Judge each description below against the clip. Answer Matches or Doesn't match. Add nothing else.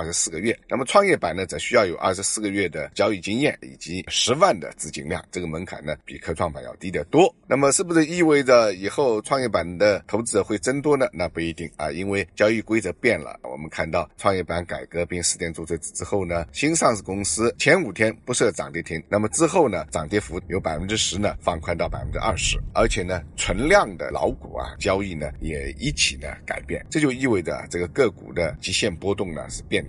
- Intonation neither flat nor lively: Matches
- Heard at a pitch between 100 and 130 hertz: Doesn't match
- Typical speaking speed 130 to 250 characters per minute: Doesn't match